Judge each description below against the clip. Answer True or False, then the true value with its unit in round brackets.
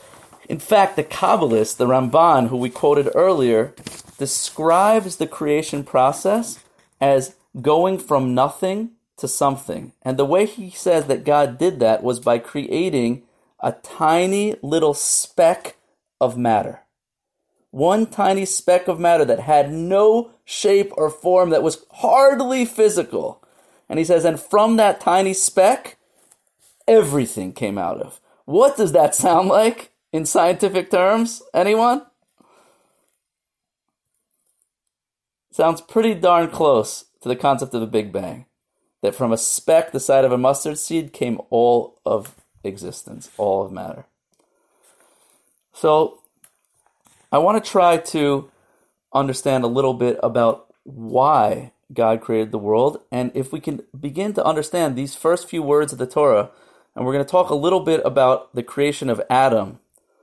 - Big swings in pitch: True (6.4 semitones)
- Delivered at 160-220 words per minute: False (145 wpm)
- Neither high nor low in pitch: True (155 Hz)